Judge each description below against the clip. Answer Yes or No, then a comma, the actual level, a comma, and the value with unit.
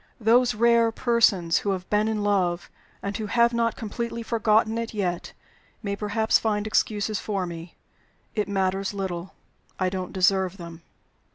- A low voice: No, high, 205 Hz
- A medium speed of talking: Yes, average, 155 wpm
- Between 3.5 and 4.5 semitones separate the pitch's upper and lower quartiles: No, average, 3.1 semitones